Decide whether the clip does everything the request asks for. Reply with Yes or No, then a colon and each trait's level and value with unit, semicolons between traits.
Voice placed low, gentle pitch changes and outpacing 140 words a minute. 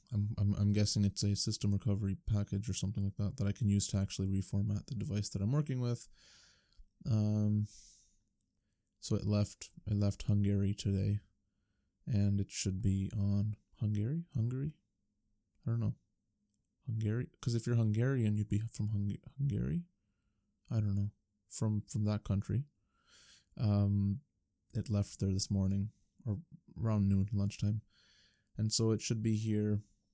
Yes: low, 105 Hz; narrow, 1.4 semitones; average, 155 wpm